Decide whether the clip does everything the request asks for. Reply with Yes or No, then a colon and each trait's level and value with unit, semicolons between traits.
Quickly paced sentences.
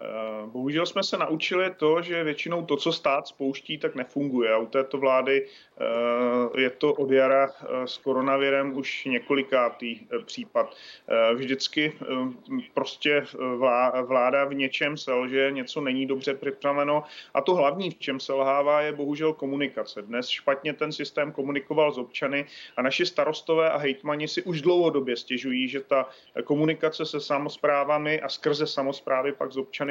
No: average, 140 wpm